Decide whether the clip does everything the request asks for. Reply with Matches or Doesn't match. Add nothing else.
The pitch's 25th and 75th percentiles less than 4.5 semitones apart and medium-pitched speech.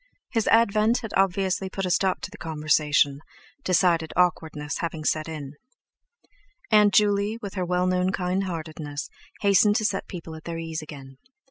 Matches